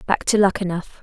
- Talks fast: No, average, 175 wpm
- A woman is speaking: Yes, female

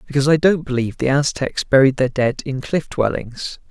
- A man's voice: Yes, male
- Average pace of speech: Yes, average, 195 wpm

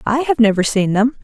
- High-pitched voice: Yes, high, 235 Hz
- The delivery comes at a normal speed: No, fast, 245 wpm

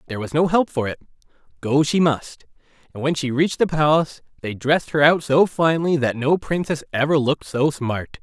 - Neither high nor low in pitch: Yes, medium, 145 Hz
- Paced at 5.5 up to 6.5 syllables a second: Yes, 5.7 syllables/s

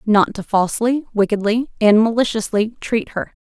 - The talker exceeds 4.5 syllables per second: Yes, 4.9 syllables/s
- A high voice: Yes, high, 220 Hz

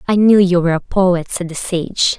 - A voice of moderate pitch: Yes, medium, 180 Hz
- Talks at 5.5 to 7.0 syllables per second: No, 4.9 syllables/s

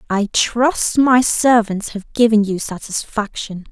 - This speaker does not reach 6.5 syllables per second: Yes, 3.7 syllables/s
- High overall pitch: Yes, high, 220 Hz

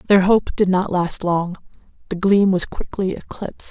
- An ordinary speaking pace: Yes, average, 180 wpm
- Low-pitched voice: No, high, 190 Hz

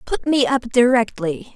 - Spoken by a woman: Yes, female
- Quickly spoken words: No, average, 155 wpm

